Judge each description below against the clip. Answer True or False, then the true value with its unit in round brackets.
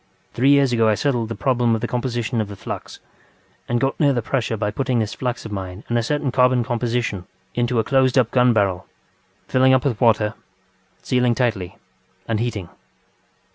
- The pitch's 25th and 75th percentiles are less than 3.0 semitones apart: True (2.6 semitones)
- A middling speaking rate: True (190 wpm)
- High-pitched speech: False (120 Hz)